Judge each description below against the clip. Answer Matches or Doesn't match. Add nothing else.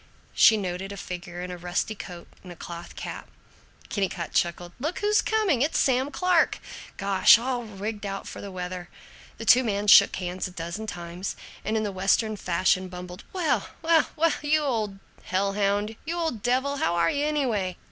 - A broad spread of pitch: Matches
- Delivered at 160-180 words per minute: Doesn't match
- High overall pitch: Matches